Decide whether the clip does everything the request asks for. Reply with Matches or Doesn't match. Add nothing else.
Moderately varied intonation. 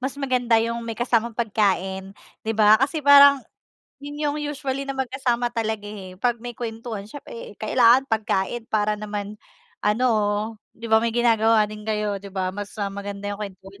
Matches